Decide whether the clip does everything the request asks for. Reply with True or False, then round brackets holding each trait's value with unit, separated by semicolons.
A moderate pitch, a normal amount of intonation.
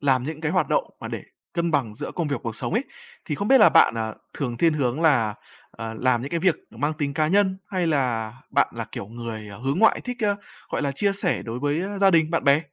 False (150 Hz; 6.7 semitones)